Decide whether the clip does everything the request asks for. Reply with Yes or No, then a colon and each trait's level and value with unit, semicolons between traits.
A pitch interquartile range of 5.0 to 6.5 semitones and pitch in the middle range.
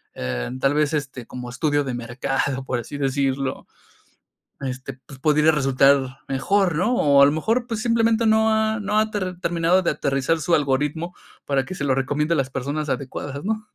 Yes: wide, 5.4 semitones; medium, 145 Hz